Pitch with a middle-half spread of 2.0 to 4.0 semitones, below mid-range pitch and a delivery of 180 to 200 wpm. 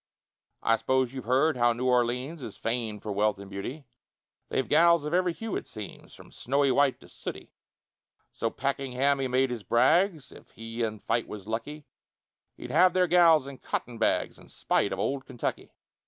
No: average, 4.5 semitones; low, 130 Hz; average, 185 wpm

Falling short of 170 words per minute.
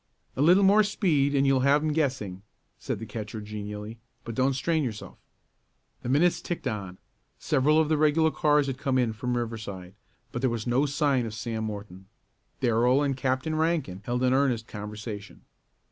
No: average, 175 wpm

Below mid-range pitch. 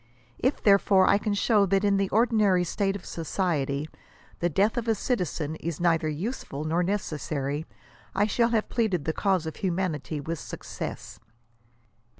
No: medium, 185 Hz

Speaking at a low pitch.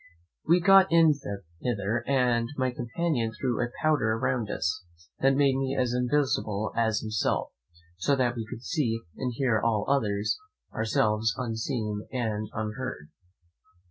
Yes: low, 120 Hz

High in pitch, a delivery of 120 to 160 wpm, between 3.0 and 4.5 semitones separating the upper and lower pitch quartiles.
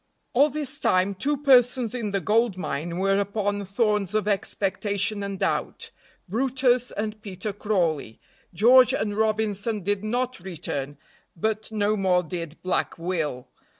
Yes: high, 205 Hz; average, 140 wpm; average, 3.5 semitones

